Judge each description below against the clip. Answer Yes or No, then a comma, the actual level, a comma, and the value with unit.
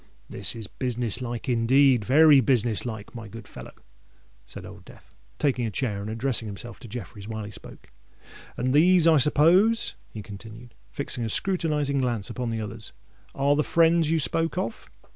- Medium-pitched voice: No, low, 125 Hz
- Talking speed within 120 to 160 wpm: No, average, 170 wpm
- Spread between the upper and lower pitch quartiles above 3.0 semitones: Yes, average, 4.9 semitones